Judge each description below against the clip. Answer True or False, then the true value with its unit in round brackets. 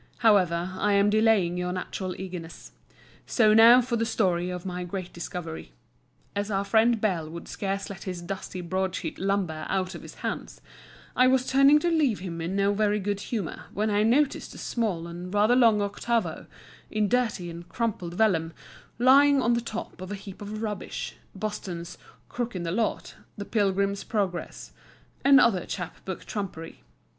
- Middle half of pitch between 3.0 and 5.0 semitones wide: True (3.8 semitones)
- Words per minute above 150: True (170 wpm)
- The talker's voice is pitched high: True (200 Hz)